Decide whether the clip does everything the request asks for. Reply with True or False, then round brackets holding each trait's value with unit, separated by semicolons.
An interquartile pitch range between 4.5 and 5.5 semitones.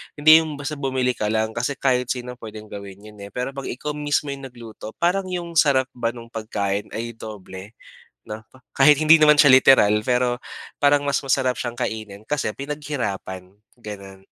True (4.8 semitones)